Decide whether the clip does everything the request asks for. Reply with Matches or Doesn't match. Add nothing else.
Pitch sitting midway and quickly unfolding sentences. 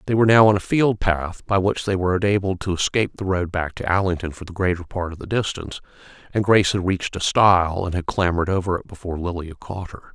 Doesn't match